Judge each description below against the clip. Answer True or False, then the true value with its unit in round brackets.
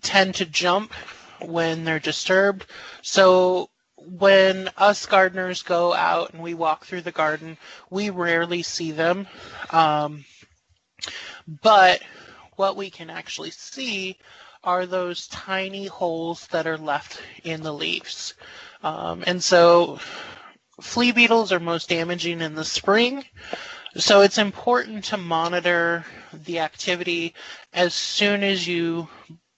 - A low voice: False (175 Hz)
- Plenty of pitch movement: False (2.9 semitones)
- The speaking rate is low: True (125 wpm)